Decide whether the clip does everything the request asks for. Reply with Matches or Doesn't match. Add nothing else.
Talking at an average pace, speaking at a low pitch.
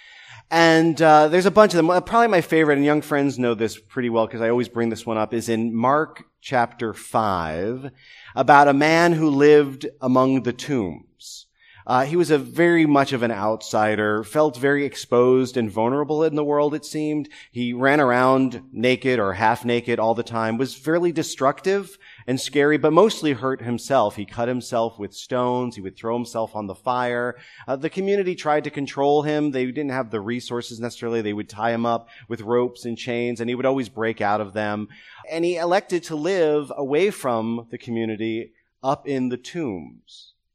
Matches